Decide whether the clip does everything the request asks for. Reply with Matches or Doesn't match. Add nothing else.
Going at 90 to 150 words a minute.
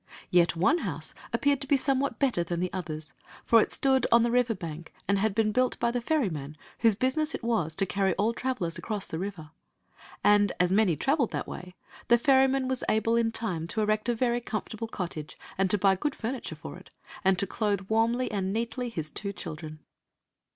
Doesn't match